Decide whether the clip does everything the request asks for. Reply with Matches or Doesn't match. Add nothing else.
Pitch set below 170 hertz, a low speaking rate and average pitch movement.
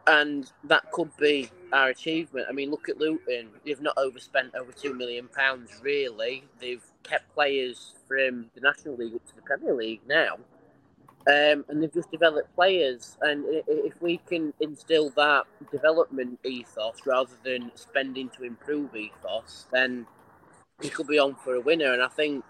Doesn't match